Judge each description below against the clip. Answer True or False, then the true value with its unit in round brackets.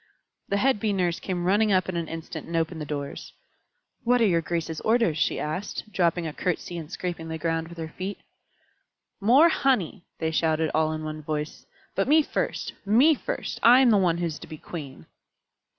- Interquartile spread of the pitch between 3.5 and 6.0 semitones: True (4.2 semitones)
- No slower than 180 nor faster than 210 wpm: True (200 wpm)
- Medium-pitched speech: True (170 Hz)